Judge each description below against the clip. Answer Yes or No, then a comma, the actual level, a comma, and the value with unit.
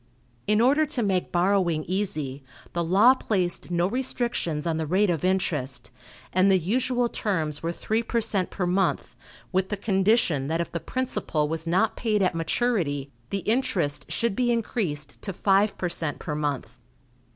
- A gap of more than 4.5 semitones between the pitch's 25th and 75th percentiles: Yes, average, 5.1 semitones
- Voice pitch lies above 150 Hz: Yes, medium, 185 Hz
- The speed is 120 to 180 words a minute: Yes, average, 170 wpm